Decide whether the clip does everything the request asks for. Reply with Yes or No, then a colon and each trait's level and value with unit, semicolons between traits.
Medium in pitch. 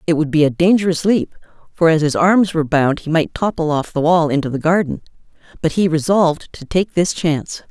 Yes: medium, 165 Hz